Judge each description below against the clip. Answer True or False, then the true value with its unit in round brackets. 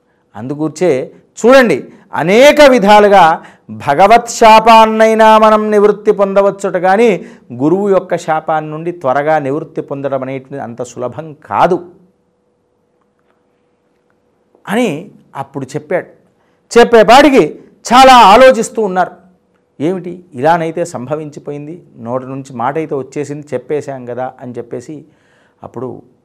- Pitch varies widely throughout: True (7.1 semitones)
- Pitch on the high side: False (165 Hz)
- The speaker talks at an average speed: True (90 wpm)